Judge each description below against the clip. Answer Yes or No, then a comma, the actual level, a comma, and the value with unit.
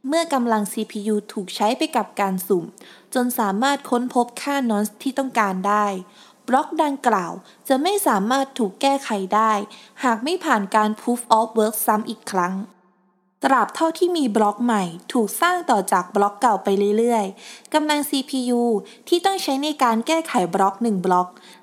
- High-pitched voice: Yes, high, 225 Hz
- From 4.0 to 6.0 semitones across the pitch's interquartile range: Yes, average, 4.7 semitones